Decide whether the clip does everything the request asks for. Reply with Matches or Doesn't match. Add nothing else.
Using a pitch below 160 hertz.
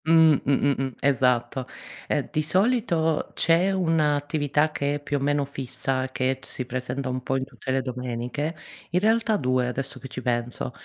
Matches